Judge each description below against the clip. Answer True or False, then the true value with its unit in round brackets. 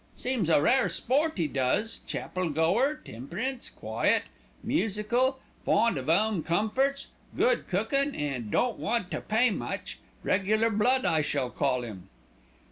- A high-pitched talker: True (210 Hz)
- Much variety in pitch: True (8.1 semitones)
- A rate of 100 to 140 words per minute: True (135 wpm)